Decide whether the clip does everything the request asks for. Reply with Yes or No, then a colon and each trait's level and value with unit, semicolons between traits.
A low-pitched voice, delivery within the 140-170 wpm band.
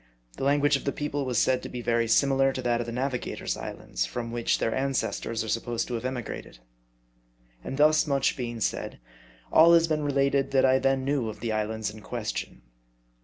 No: low, 130 Hz; average, 200 wpm